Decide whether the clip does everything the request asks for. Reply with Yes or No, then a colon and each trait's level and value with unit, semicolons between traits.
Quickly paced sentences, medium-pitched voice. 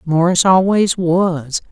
No: slow, 105 wpm; medium, 175 Hz